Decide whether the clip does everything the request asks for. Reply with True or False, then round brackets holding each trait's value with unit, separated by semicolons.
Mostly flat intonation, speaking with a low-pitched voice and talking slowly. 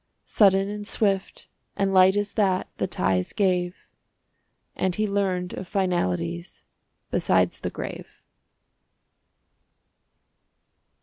False (2.0 semitones; 190 Hz; 100 wpm)